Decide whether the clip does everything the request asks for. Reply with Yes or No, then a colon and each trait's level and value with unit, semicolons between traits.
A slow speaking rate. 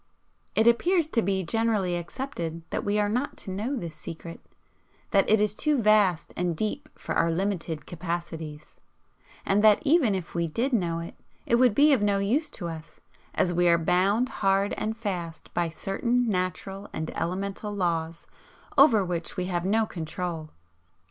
No: average, 170 wpm